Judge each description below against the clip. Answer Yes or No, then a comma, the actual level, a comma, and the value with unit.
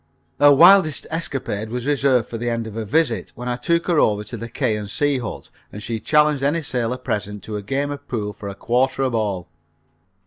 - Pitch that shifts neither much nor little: Yes, average, 4.9 semitones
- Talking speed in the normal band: No, fast, 220 wpm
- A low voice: Yes, low, 125 Hz